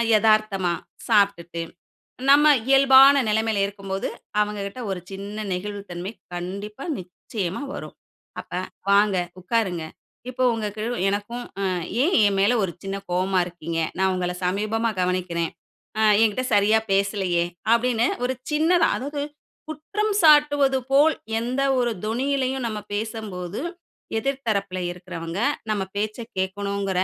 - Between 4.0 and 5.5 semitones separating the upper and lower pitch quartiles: Yes, average, 4.4 semitones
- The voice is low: No, high, 205 Hz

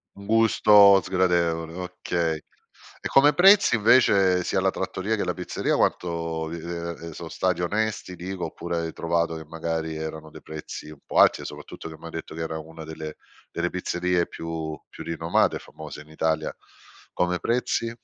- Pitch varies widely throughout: No, narrow, 2.5 semitones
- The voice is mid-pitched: No, very low, 85 Hz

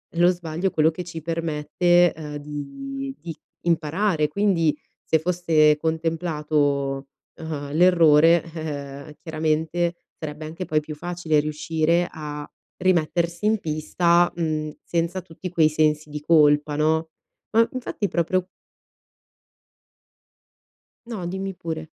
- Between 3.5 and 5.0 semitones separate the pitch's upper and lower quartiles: No, narrow, 2.4 semitones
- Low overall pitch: No, medium, 160 Hz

